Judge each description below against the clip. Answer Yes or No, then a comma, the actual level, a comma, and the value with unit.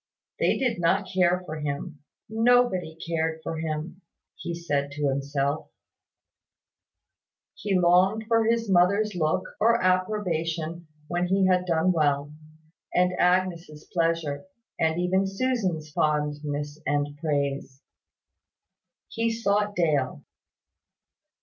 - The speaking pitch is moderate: Yes, medium, 170 Hz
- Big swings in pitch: No, average, 4.0 semitones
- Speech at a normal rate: No, slow, 110 wpm